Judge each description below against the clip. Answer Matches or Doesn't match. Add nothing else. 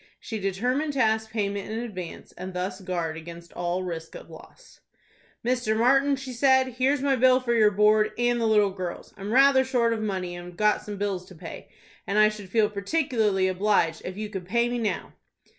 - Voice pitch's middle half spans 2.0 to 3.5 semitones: Doesn't match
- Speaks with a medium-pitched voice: Doesn't match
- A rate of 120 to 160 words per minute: Doesn't match